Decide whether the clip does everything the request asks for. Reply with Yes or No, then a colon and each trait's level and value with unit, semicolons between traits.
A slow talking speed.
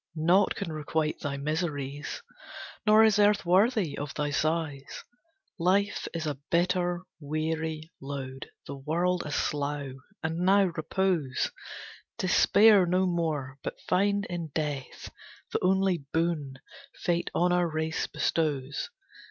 Yes: slow, 125 wpm